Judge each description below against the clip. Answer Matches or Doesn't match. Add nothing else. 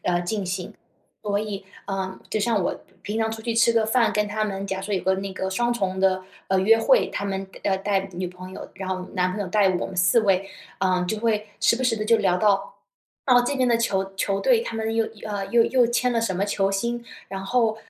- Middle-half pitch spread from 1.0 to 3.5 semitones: Matches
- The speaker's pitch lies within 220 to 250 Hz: Doesn't match